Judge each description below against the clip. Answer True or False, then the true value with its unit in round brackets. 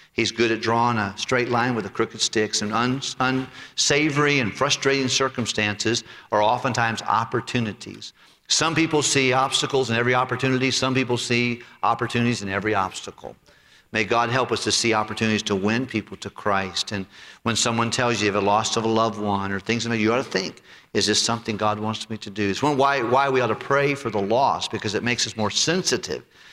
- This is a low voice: True (115 Hz)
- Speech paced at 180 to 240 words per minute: True (195 wpm)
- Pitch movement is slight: False (3.4 semitones)